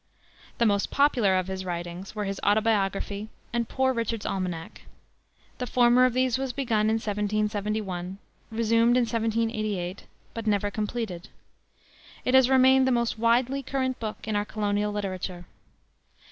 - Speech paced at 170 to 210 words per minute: No, average, 145 wpm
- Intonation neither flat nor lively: Yes, average, 3.0 semitones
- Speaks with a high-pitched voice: Yes, high, 215 Hz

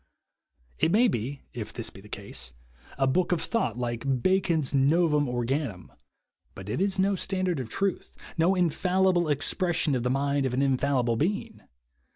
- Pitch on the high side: No, medium, 145 Hz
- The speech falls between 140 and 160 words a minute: No, average, 175 wpm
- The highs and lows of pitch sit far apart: Yes, wide, 6.4 semitones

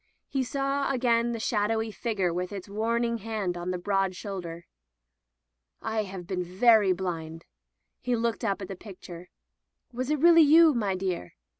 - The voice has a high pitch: Yes, high, 205 Hz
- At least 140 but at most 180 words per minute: Yes, average, 165 wpm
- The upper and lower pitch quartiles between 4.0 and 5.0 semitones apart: Yes, average, 4.6 semitones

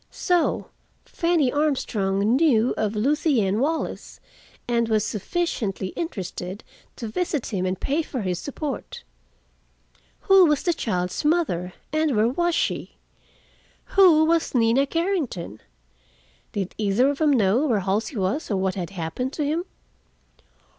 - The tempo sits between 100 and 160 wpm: Yes, slow, 135 wpm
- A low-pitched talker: No, high, 245 Hz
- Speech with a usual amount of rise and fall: No, wide, 7.9 semitones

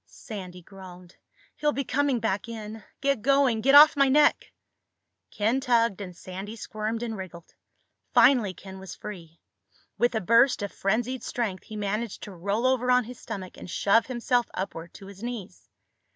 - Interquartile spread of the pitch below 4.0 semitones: No, average, 4.4 semitones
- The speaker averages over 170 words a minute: No, average, 165 wpm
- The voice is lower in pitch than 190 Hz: No, high, 220 Hz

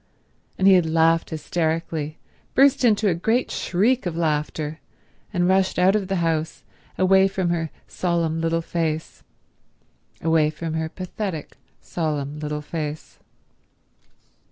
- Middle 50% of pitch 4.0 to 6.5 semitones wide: No, average, 3.0 semitones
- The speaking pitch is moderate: Yes, medium, 165 Hz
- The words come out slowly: Yes, slow, 125 wpm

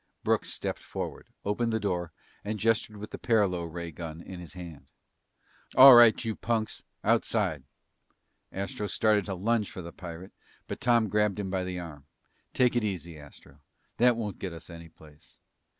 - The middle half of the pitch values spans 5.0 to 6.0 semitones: No, average, 4.4 semitones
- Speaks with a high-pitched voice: No, very low, 95 Hz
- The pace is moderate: Yes, average, 170 wpm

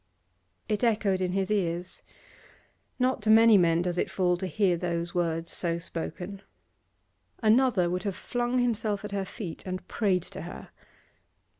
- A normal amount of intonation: Yes, average, 3.6 semitones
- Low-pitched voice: No, high, 190 Hz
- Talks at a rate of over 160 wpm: No, average, 155 wpm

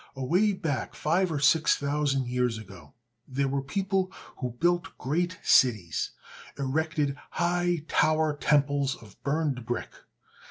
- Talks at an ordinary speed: No, slow, 125 wpm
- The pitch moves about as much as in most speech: Yes, average, 4.1 semitones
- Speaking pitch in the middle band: Yes, medium, 145 Hz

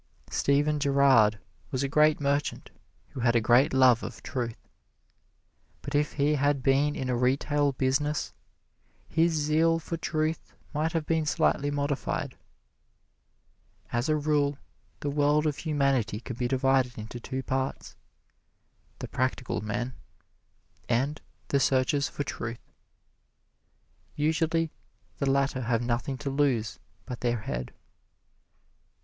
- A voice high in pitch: No, medium, 140 Hz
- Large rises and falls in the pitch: No, average, 2.9 semitones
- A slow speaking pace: Yes, slow, 130 wpm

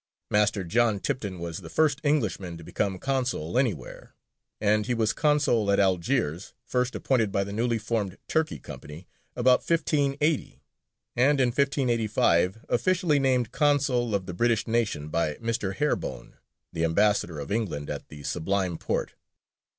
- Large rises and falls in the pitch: Yes, wide, 5.9 semitones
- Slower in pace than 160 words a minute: Yes, average, 145 wpm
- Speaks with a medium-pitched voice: No, low, 115 Hz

